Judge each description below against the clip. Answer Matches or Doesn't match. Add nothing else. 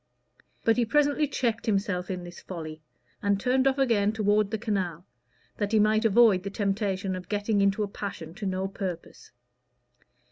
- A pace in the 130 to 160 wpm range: Doesn't match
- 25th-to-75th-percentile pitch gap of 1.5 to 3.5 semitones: Matches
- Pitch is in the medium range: Doesn't match